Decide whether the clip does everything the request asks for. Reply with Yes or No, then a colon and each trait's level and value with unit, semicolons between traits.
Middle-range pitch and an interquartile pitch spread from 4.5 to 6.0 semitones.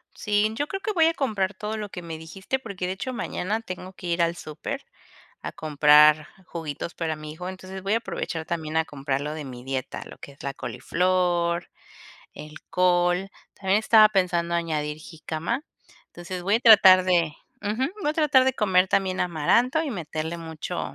Yes: medium, 180 Hz; average, 4.8 semitones